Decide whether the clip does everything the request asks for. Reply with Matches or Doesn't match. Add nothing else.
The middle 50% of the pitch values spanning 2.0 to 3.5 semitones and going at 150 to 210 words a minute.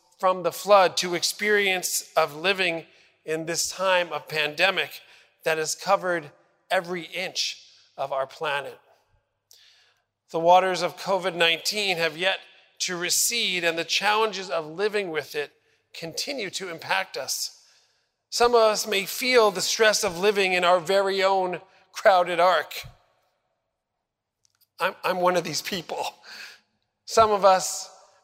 Doesn't match